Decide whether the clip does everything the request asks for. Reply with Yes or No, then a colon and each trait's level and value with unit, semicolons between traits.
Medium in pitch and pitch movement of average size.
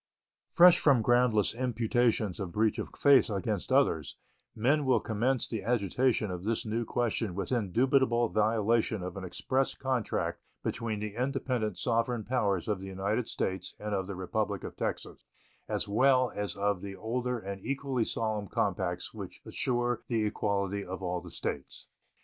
No: low, 110 Hz; average, 3.7 semitones